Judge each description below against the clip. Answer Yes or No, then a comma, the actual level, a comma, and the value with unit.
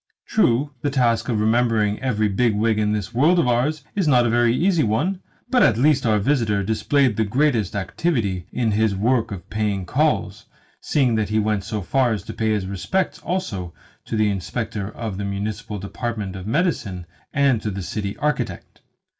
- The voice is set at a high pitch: No, low, 110 Hz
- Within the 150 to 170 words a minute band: No, average, 190 wpm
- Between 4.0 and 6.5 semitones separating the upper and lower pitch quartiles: Yes, average, 4.3 semitones